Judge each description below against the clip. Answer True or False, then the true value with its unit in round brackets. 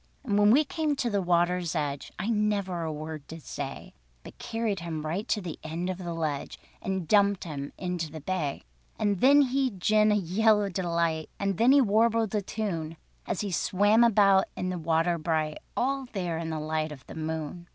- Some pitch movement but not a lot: True (4.6 semitones)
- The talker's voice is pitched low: False (180 Hz)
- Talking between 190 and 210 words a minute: True (205 wpm)